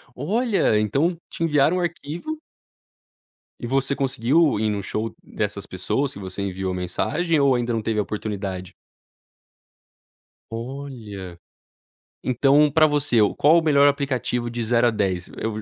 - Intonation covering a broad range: Yes, wide, 5.7 semitones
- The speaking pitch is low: Yes, low, 125 Hz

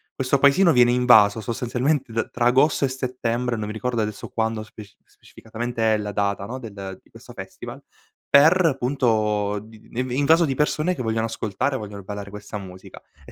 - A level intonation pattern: No, average, 3.6 semitones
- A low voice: Yes, low, 115 Hz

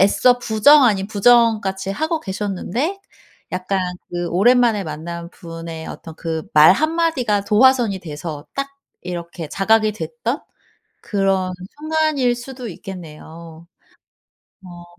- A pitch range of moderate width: No, wide, 6.2 semitones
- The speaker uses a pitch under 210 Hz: Yes, high, 195 Hz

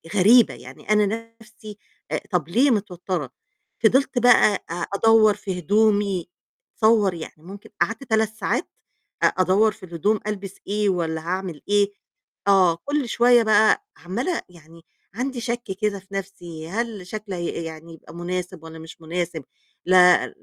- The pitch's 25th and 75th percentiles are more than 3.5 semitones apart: Yes, average, 4.0 semitones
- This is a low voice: No, high, 200 Hz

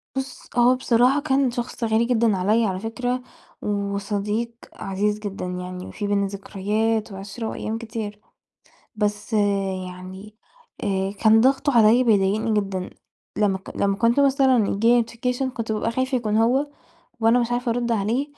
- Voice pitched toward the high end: Yes, high, 220 Hz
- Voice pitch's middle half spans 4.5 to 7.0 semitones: No, average, 3.3 semitones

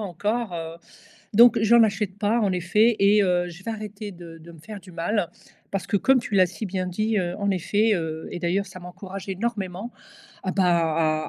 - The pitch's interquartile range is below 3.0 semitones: No, average, 3.4 semitones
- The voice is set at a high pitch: Yes, high, 195 Hz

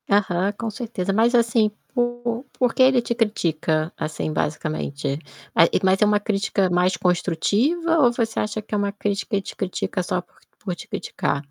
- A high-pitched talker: Yes, high, 205 Hz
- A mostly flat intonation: No, average, 4.7 semitones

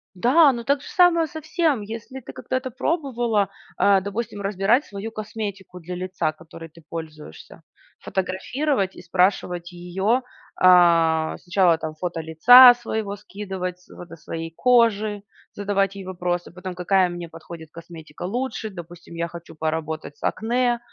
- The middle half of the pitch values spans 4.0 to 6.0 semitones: Yes, average, 5.2 semitones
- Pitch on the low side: No, high, 190 Hz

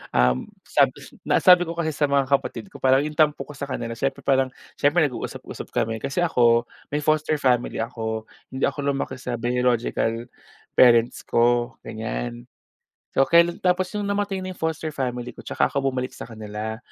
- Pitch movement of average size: Yes, average, 4.6 semitones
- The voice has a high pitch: No, low, 130 Hz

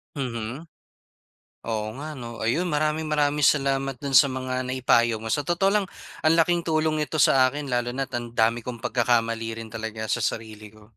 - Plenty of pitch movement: No, average, 4.4 semitones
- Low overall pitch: Yes, low, 130 Hz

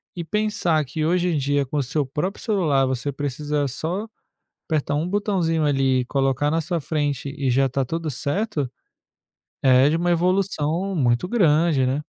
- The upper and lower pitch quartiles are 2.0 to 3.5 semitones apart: No, average, 4.1 semitones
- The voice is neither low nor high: Yes, medium, 150 Hz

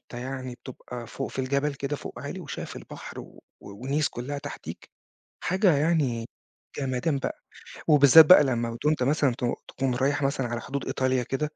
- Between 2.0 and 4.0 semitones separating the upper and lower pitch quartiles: Yes, average, 2.7 semitones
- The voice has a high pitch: No, low, 135 Hz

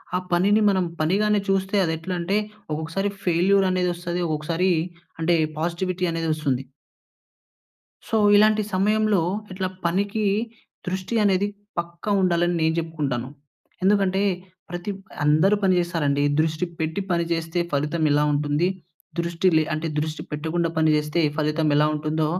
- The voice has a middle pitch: Yes, medium, 170 Hz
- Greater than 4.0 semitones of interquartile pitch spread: No, average, 3.2 semitones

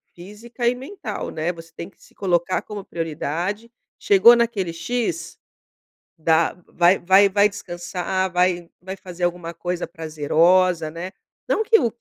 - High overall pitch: No, medium, 180 Hz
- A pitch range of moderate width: Yes, average, 3.2 semitones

